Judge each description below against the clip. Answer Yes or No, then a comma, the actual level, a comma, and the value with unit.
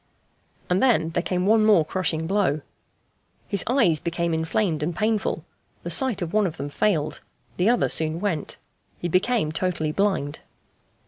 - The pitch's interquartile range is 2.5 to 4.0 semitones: No, average, 4.6 semitones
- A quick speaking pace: No, average, 155 wpm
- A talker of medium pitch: Yes, medium, 180 Hz